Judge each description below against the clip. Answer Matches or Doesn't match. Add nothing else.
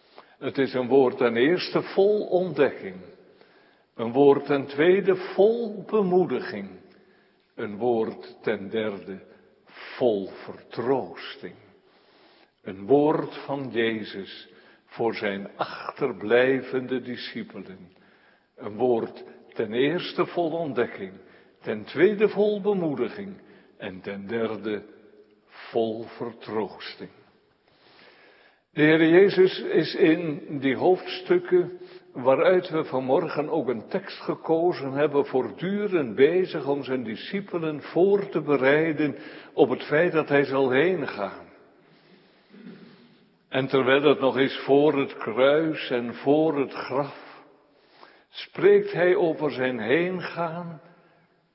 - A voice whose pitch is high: Doesn't match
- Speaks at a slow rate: Matches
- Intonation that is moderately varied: Doesn't match